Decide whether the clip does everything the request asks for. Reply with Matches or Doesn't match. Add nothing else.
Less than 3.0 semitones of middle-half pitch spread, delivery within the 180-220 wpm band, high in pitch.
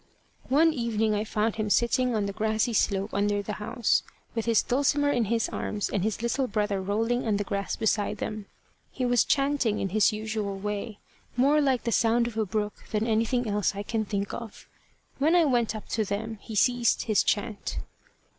Matches